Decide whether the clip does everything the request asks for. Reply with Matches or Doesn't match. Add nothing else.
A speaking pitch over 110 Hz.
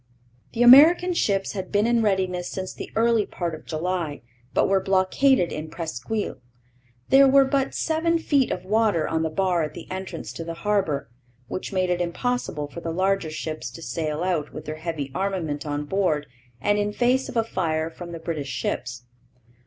Matches